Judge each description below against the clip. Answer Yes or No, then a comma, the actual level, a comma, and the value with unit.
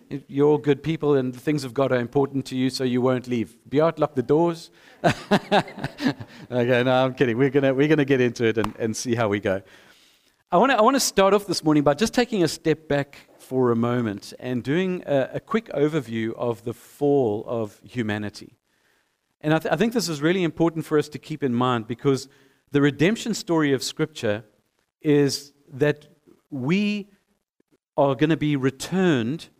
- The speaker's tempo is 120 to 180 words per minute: No, average, 195 wpm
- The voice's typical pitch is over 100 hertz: Yes, medium, 140 Hz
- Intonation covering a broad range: No, average, 4.0 semitones